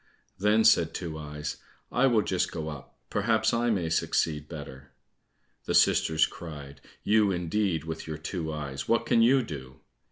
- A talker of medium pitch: No, very low, 80 Hz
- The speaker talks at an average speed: Yes, average, 160 wpm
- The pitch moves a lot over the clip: Yes, wide, 5.9 semitones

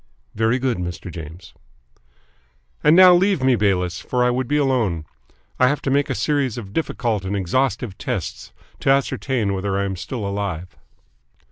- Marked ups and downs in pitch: Yes, wide, 5.8 semitones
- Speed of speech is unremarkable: Yes, average, 165 wpm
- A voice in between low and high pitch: No, low, 115 Hz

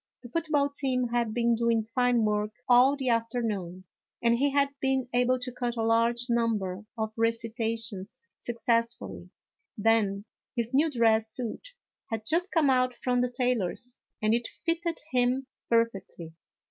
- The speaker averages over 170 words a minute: No, average, 150 wpm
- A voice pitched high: Yes, high, 235 Hz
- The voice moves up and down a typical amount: No, narrow, 2.1 semitones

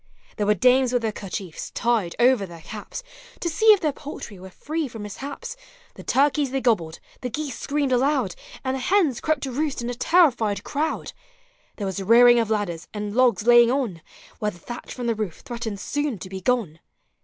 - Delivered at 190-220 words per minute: Yes, average, 200 wpm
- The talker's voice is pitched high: Yes, high, 240 Hz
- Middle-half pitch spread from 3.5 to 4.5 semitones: No, average, 5.1 semitones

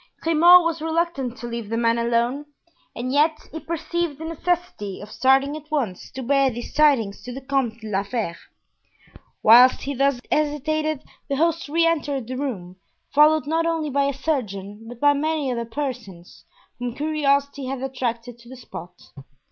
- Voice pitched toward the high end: Yes, very high, 275 Hz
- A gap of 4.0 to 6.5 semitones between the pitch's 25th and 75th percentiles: Yes, average, 4.5 semitones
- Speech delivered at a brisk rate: No, average, 170 wpm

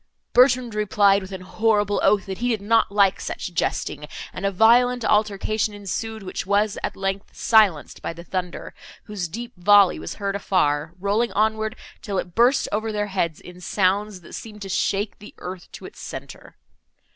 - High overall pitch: Yes, high, 205 Hz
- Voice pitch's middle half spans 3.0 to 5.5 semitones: No, narrow, 2.6 semitones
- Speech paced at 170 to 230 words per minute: Yes, average, 180 wpm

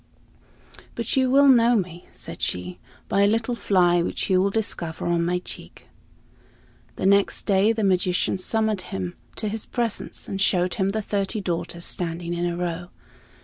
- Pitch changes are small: No, average, 3.8 semitones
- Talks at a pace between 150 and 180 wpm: Yes, average, 170 wpm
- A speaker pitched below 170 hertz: No, high, 190 Hz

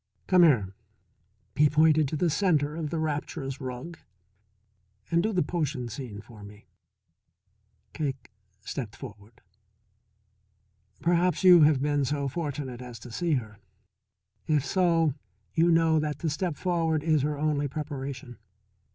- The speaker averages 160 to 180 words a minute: No, slow, 135 wpm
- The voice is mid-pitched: Yes, medium, 150 Hz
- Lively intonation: No, average, 4.0 semitones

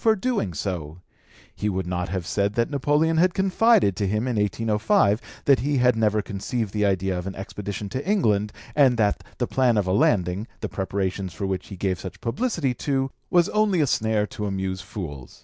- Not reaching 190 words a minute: No, average, 200 wpm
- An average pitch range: No, wide, 5.8 semitones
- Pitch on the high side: No, low, 105 Hz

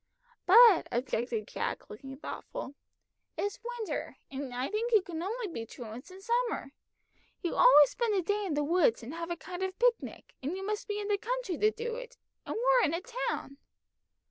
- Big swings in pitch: Yes, wide, 8.1 semitones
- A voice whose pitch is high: Yes, very high, 380 Hz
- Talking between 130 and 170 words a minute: No, average, 195 wpm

